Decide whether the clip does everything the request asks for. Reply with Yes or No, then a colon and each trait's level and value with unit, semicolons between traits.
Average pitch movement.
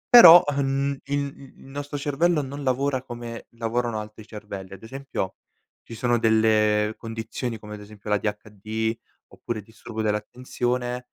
Yes: average, 4.0 semitones